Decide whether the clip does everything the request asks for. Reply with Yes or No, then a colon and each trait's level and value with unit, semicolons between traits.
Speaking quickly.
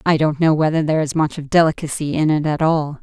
Yes: fast, 260 wpm